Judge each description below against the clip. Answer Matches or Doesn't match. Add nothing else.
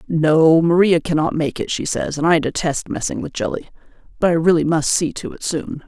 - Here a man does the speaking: Doesn't match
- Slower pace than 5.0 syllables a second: Doesn't match